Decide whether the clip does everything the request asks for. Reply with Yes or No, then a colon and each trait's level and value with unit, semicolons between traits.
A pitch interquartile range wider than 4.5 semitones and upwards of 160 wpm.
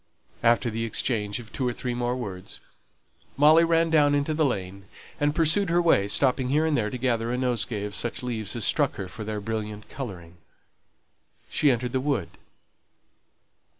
Yes: average, 5.2 semitones; average, 180 wpm